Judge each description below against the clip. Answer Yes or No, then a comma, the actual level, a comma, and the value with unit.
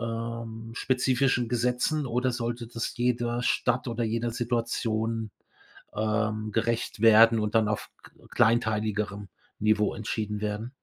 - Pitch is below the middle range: Yes, low, 115 Hz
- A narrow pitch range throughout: Yes, narrow, 1.8 semitones